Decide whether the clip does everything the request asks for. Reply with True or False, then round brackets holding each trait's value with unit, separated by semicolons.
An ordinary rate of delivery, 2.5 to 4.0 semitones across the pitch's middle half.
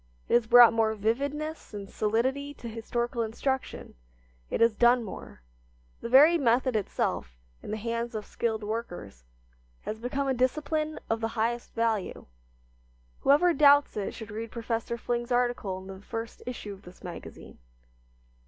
True (155 wpm; 2.8 semitones)